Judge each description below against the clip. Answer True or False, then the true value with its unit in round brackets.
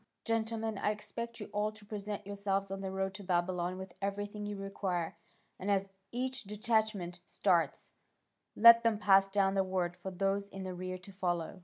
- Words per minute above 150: True (180 wpm)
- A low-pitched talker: False (195 Hz)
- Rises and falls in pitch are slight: True (2.0 semitones)